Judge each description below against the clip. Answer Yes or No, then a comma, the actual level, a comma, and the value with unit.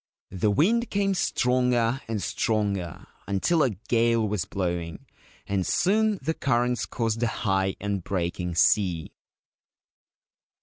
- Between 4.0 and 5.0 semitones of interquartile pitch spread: Yes, average, 4.6 semitones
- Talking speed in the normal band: No, slow, 120 wpm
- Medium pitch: No, low, 110 Hz